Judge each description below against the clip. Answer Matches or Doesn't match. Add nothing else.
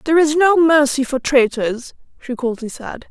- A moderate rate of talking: Matches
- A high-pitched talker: Matches